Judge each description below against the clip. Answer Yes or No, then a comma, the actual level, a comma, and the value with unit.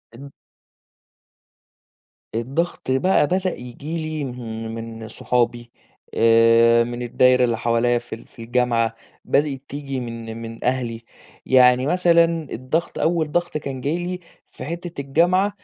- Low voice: Yes, low, 125 Hz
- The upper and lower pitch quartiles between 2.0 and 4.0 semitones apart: No, average, 5.2 semitones